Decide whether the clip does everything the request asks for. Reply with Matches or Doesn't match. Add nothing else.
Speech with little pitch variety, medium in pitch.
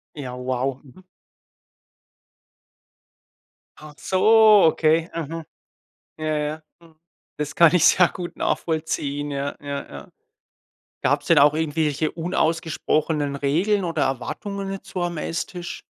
Doesn't match